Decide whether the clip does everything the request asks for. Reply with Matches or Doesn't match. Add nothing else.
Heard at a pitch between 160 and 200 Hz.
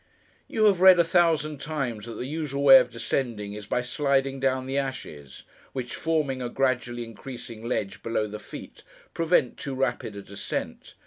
Doesn't match